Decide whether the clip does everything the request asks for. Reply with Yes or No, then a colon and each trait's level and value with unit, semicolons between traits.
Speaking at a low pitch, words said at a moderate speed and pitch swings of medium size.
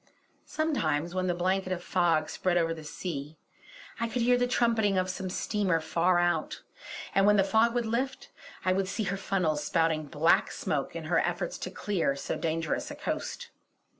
No: medium, 185 Hz; average, 185 wpm; average, 4.1 semitones